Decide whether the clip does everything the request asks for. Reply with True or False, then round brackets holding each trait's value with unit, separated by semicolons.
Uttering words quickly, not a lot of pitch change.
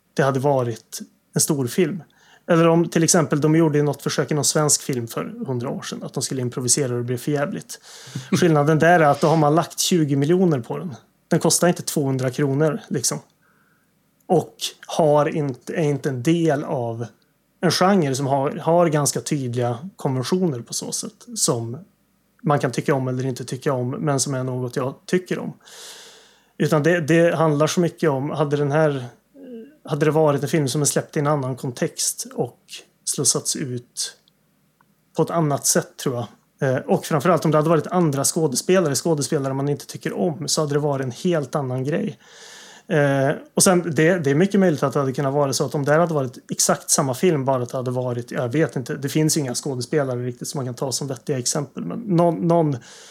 False (200 wpm; 3.7 semitones)